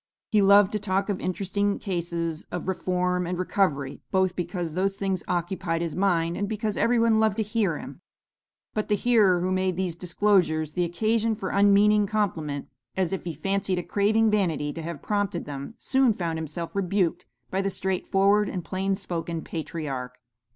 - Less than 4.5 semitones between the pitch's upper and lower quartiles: Yes, average, 3.1 semitones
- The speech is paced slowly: No, average, 175 wpm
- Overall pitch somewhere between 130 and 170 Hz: No, medium, 185 Hz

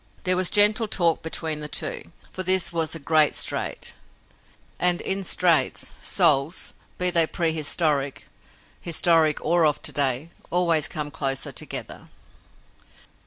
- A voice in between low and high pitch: Yes, medium, 165 Hz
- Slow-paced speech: Yes, slow, 130 wpm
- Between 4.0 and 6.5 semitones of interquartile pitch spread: No, average, 3.0 semitones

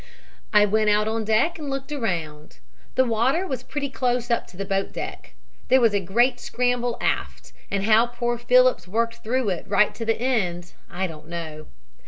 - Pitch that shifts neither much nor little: Yes, average, 4.2 semitones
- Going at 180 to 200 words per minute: Yes, average, 190 wpm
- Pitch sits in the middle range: No, high, 225 Hz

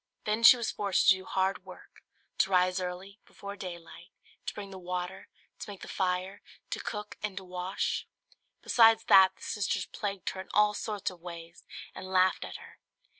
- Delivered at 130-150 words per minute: No, average, 185 wpm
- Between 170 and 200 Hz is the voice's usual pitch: Yes, high, 190 Hz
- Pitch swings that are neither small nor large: No, narrow, 1.9 semitones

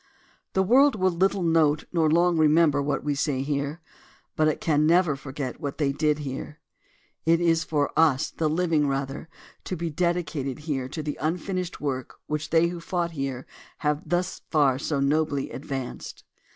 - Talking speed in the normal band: Yes, average, 170 wpm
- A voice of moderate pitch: Yes, medium, 155 Hz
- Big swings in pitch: No, average, 3.0 semitones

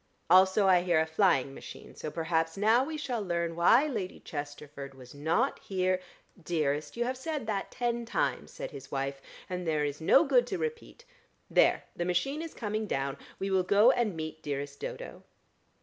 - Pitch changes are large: Yes, wide, 7.4 semitones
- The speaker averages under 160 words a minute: No, average, 185 wpm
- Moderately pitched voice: Yes, medium, 180 Hz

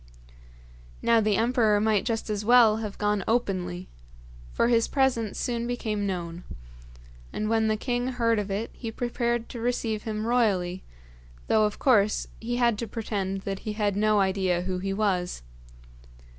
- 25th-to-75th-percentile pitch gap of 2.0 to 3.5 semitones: Yes, average, 2.9 semitones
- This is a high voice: Yes, high, 215 Hz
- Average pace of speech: Yes, average, 160 wpm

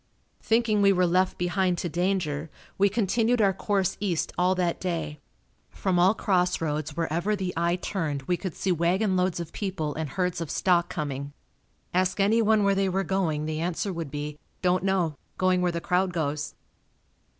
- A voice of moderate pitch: Yes, medium, 180 Hz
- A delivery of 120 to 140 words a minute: No, average, 180 wpm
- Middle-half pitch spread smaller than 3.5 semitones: Yes, average, 2.9 semitones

